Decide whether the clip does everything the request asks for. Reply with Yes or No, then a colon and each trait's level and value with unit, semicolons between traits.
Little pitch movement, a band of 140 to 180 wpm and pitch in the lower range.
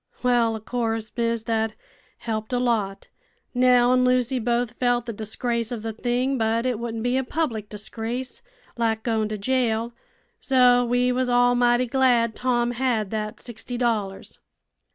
No: narrow, 1.9 semitones; average, 160 wpm; high, 240 Hz